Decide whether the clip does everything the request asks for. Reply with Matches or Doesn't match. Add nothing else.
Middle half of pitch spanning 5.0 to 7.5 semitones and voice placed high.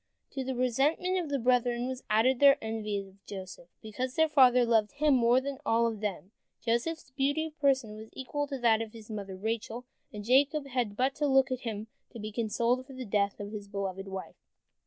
Doesn't match